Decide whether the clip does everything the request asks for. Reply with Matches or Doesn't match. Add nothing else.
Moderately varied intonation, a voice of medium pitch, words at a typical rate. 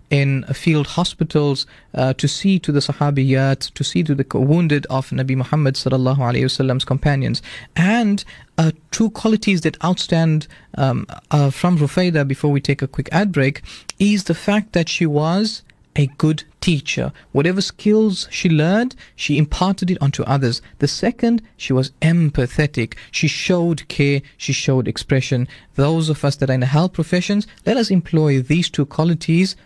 Matches